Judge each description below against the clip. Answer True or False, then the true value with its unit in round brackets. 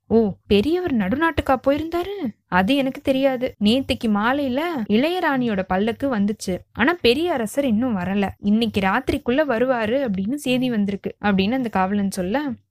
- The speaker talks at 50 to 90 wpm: False (125 wpm)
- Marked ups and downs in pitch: False (5.0 semitones)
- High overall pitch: True (240 Hz)